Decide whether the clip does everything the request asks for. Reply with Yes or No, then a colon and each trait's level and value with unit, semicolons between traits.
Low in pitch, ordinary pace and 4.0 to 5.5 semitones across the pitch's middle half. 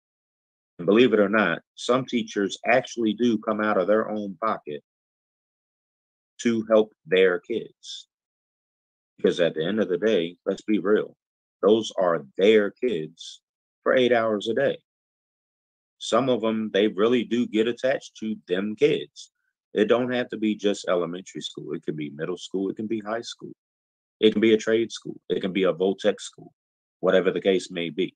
No: low, 110 Hz; average, 180 wpm; average, 2.9 semitones